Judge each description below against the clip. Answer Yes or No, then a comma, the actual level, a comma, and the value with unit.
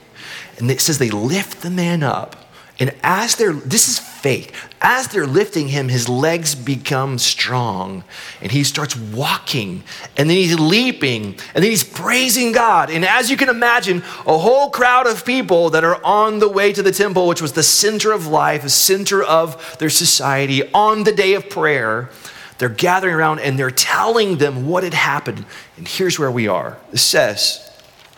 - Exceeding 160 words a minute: Yes, average, 185 wpm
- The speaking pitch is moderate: Yes, medium, 165 Hz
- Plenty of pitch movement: Yes, wide, 6.6 semitones